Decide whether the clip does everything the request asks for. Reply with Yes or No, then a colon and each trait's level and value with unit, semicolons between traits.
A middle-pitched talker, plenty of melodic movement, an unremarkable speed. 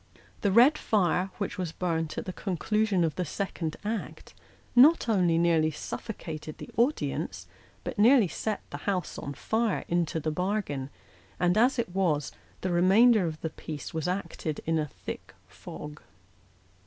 No: medium, 180 Hz; average, 4.9 semitones; average, 155 wpm